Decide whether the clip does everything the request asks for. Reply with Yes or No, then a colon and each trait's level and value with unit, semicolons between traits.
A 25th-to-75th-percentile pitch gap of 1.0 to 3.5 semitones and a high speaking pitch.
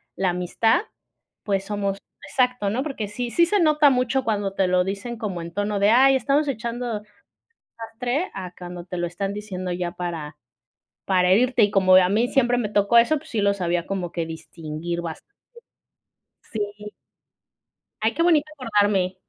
No: average, 5.1 semitones; high, 205 Hz